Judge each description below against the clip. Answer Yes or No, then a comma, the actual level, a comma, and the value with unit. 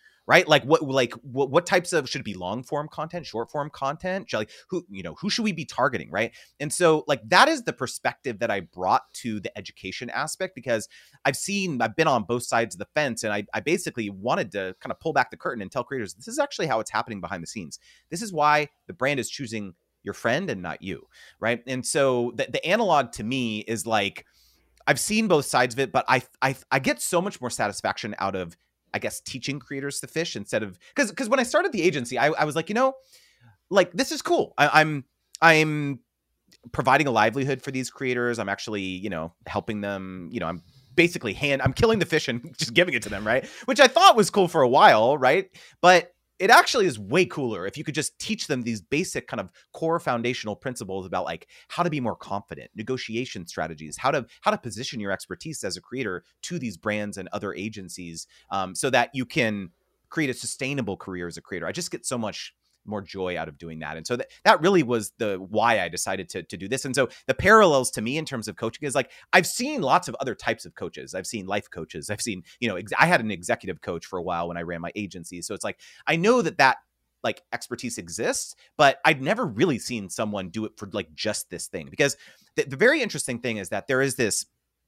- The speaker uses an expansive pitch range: Yes, wide, 7.2 semitones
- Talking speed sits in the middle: No, fast, 240 wpm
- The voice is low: Yes, low, 125 Hz